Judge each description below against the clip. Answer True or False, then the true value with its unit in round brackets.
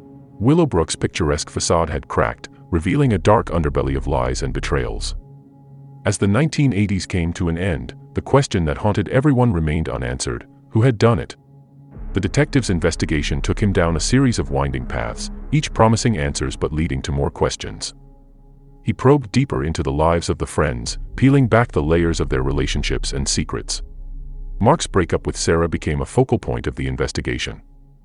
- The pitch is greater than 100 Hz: False (95 Hz)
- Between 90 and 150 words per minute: False (170 wpm)